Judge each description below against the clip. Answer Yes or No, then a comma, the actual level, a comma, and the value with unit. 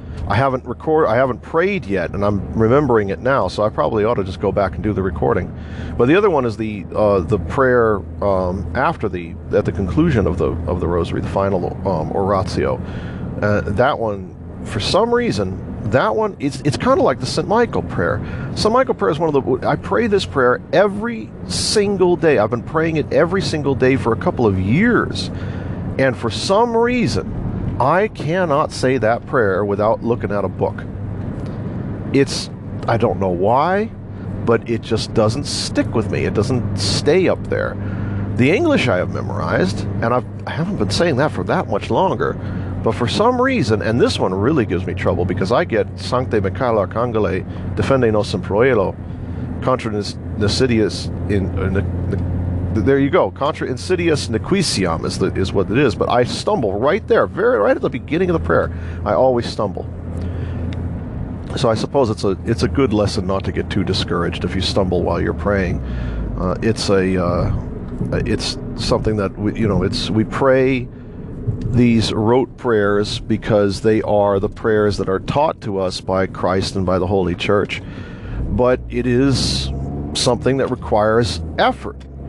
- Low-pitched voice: Yes, low, 105 Hz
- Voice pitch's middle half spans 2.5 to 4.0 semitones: No, average, 4.6 semitones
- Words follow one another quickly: No, average, 185 wpm